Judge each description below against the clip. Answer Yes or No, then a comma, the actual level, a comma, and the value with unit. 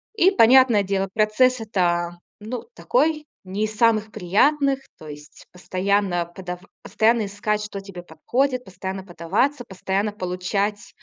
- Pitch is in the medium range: No, high, 205 Hz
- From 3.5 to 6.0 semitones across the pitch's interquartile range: Yes, average, 4.1 semitones